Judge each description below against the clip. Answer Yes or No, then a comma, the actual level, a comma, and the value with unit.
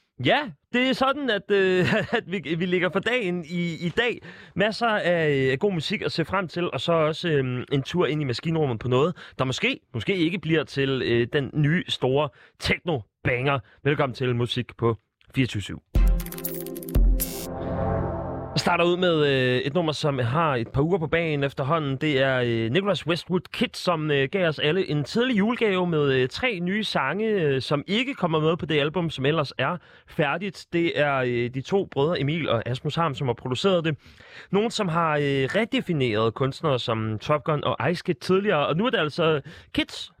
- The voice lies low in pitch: No, medium, 155 Hz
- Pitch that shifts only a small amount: No, average, 5.2 semitones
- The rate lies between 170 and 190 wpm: Yes, average, 185 wpm